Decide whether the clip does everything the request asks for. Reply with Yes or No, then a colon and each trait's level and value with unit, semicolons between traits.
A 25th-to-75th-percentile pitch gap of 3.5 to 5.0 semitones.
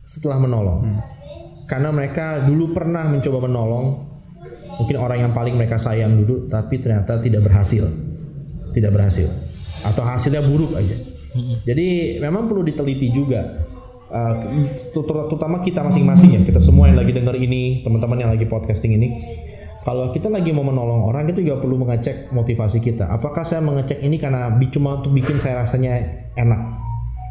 Yes: average, 4.5 semitones